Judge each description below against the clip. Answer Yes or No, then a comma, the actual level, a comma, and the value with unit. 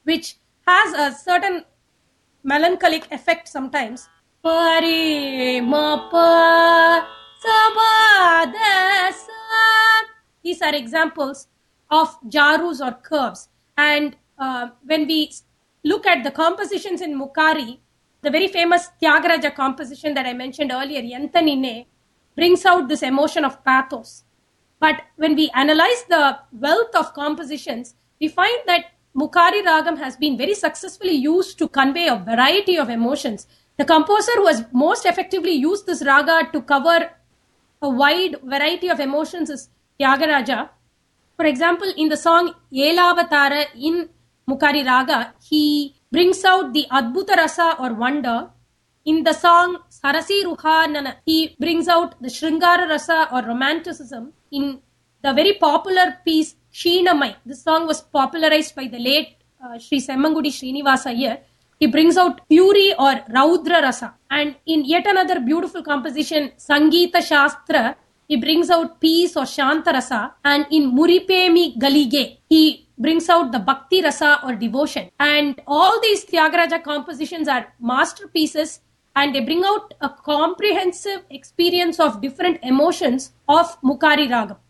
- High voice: Yes, very high, 310 Hz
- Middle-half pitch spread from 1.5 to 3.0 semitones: No, average, 3.5 semitones